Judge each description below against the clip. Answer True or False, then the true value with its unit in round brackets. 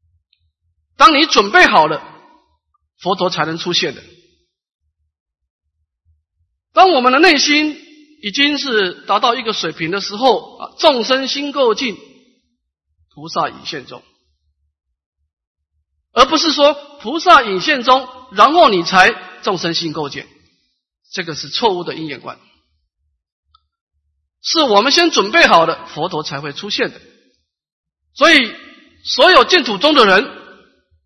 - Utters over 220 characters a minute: False (180 characters per minute)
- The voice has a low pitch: False (165 Hz)